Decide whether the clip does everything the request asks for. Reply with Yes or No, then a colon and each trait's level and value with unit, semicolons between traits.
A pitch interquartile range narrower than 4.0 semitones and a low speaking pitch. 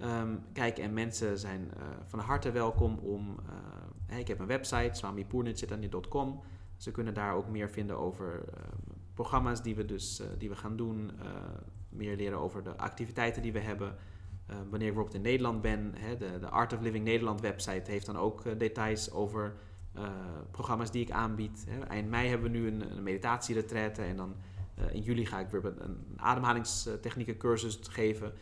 Yes: average, 3.0 semitones; low, 105 Hz